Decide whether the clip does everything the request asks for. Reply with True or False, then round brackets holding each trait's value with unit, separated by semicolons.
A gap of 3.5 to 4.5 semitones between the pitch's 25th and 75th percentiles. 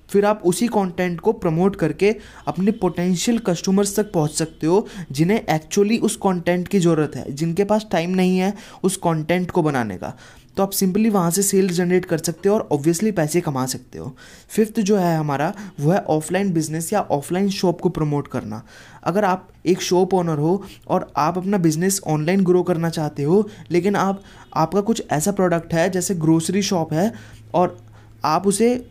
True (3.8 semitones)